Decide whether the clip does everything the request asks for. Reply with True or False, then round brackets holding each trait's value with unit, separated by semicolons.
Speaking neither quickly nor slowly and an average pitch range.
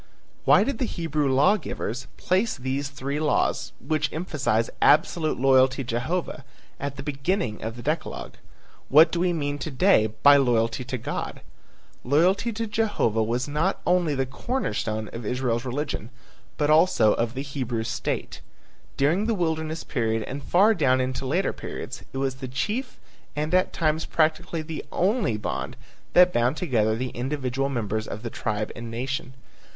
True (165 wpm; 5.0 semitones)